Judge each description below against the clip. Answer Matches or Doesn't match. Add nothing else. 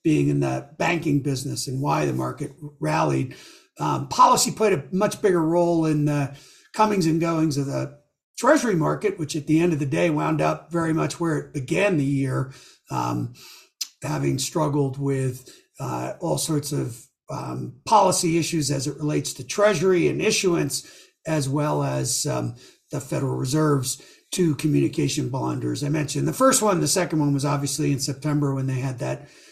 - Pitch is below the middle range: Doesn't match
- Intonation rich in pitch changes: Doesn't match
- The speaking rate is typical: Matches